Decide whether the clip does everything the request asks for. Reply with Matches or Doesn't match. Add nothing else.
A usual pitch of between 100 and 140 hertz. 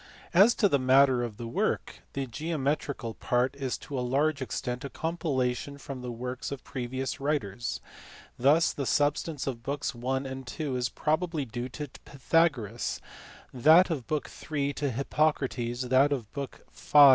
Matches